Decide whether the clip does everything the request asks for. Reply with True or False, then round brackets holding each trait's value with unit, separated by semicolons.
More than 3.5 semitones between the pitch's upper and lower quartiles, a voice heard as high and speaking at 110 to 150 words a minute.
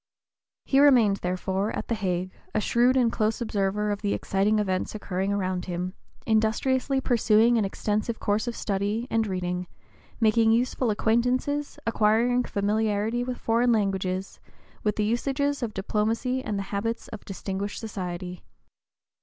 False (3.2 semitones; 215 Hz; 145 wpm)